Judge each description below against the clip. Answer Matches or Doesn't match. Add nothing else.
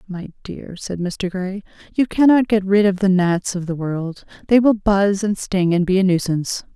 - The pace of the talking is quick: Matches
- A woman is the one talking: Matches